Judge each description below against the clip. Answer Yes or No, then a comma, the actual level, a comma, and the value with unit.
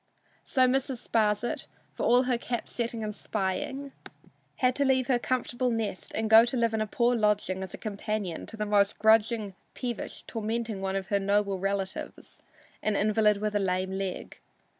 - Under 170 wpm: No, average, 175 wpm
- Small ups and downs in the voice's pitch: No, average, 3.1 semitones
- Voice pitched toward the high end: Yes, high, 215 Hz